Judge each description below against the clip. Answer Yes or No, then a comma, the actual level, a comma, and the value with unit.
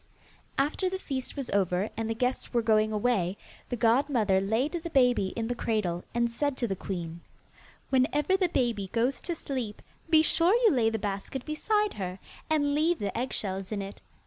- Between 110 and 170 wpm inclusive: No, average, 185 wpm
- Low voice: No, high, 240 Hz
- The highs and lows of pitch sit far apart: Yes, wide, 6.0 semitones